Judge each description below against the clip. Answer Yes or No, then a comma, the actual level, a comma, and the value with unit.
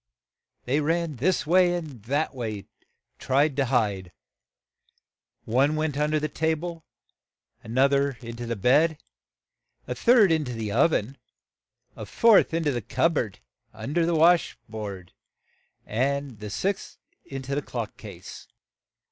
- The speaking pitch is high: No, medium, 140 Hz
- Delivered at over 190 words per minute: No, average, 165 wpm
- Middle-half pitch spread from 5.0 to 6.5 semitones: Yes, wide, 5.4 semitones